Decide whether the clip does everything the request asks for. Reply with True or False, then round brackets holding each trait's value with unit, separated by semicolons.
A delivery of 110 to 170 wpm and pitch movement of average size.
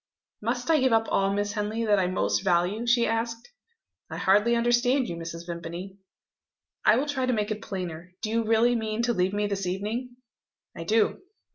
False (190 wpm; 3.7 semitones)